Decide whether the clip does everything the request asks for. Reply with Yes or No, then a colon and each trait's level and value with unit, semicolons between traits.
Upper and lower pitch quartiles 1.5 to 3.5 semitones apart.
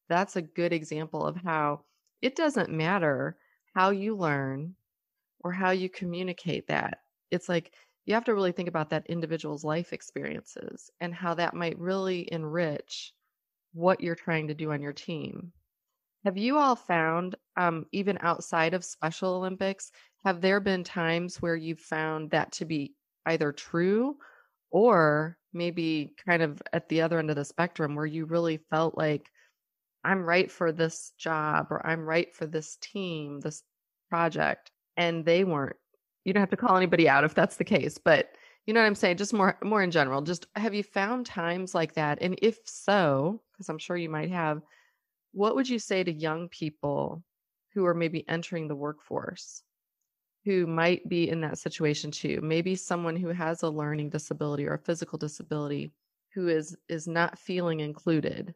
Yes: average, 2.9 semitones